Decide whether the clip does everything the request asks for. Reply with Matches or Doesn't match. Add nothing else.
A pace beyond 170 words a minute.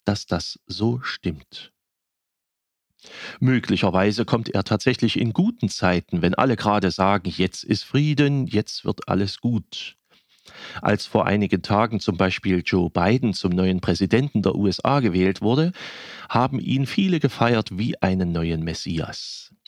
Doesn't match